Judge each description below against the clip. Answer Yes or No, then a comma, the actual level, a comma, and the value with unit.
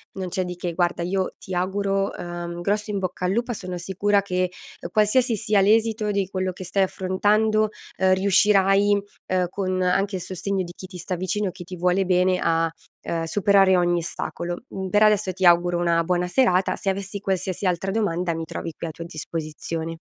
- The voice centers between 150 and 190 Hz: Yes, medium, 185 Hz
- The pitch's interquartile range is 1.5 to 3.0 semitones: Yes, narrow, 2.2 semitones